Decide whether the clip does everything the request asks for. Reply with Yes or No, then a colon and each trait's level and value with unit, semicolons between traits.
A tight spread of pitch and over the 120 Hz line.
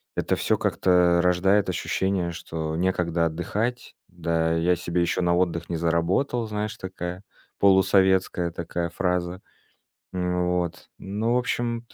No: narrow, 2.0 semitones; very low, 90 Hz